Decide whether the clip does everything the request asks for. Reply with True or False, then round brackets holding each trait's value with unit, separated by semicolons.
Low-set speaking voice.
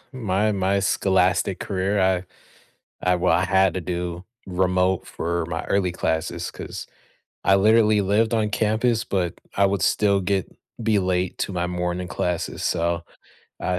True (95 Hz)